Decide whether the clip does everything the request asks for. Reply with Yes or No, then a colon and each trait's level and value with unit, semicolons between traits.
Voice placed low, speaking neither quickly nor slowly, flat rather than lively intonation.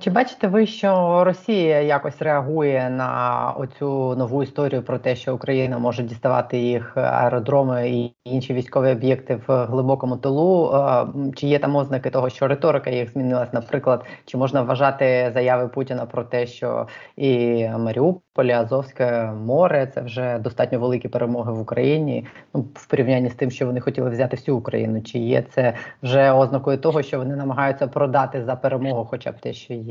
No: low, 130 Hz; fast, 170 wpm; narrow, 2.1 semitones